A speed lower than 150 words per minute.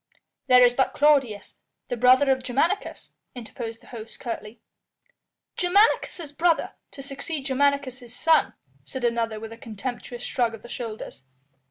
Yes: average, 140 wpm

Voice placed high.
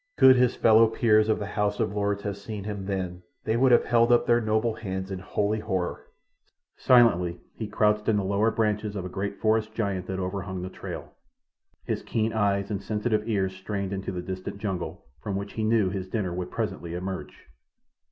No: low, 100 Hz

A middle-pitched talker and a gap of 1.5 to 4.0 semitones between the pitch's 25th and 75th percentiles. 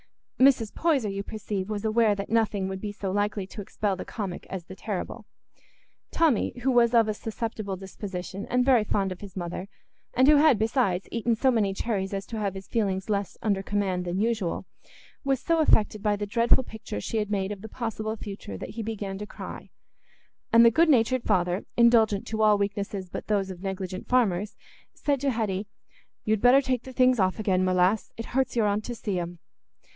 No: high, 210 Hz; average, 3.2 semitones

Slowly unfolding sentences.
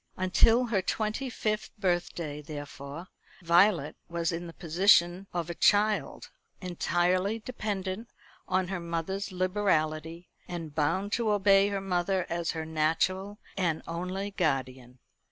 Yes: slow, 125 wpm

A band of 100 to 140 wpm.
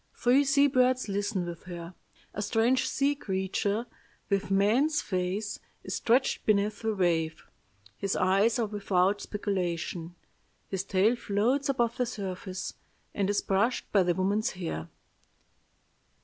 Yes: slow, 135 wpm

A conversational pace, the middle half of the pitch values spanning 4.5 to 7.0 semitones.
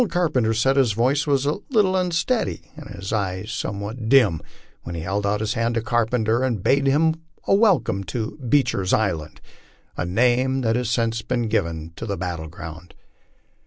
Yes: average, 170 wpm; wide, 5.5 semitones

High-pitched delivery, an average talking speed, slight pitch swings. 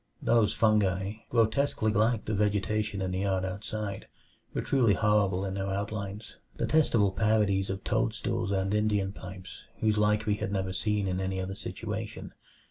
No: low, 100 Hz; average, 155 wpm; narrow, 1.9 semitones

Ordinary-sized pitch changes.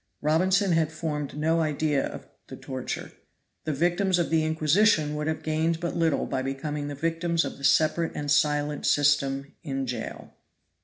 No: narrow, 2.2 semitones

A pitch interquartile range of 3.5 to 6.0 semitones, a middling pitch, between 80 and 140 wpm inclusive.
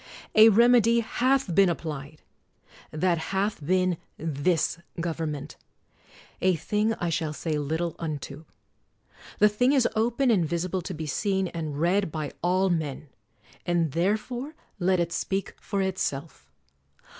Yes: average, 4.4 semitones; medium, 175 Hz; slow, 135 wpm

